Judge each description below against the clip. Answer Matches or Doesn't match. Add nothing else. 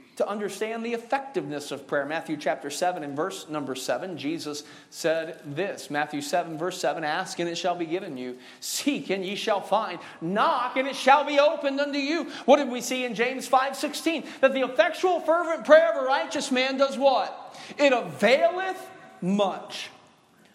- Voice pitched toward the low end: Doesn't match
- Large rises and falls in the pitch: Matches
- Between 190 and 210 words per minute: Doesn't match